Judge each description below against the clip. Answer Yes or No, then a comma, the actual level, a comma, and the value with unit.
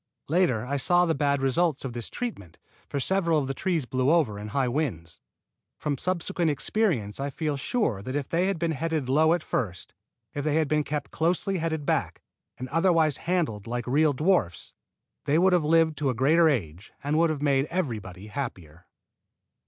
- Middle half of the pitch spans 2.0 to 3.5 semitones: No, average, 4.7 semitones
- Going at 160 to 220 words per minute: Yes, average, 190 wpm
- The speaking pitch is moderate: Yes, medium, 145 Hz